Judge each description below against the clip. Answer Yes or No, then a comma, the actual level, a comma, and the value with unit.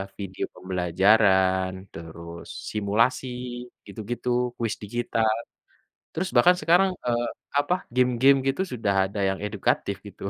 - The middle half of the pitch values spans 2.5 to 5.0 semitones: Yes, average, 4.5 semitones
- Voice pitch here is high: No, low, 110 Hz